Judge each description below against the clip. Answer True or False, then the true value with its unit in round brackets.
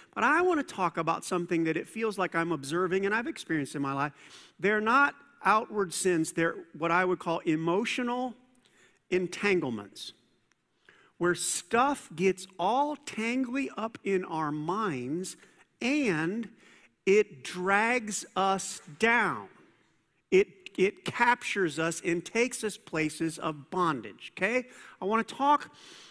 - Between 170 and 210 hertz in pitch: True (190 Hz)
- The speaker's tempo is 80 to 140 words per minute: True (135 wpm)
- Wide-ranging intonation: True (5.9 semitones)